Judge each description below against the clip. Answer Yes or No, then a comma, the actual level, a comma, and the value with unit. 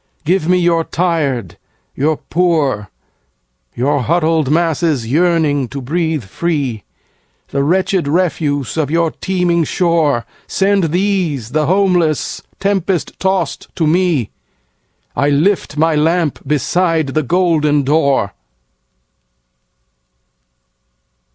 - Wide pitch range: No, average, 3.8 semitones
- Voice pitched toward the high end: No, medium, 160 Hz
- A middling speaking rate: No, slow, 90 wpm